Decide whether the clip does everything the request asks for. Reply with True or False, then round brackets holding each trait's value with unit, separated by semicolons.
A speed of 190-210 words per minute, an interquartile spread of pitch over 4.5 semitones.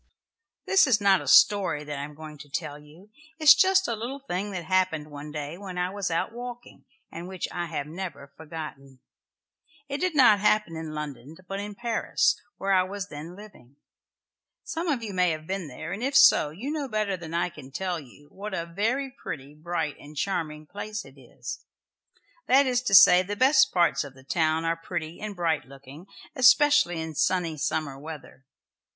True (195 wpm; 5.6 semitones)